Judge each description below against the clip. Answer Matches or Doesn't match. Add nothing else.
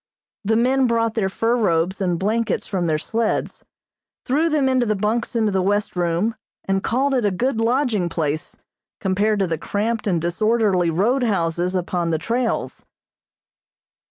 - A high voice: Matches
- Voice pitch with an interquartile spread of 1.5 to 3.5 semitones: Doesn't match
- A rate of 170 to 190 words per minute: Doesn't match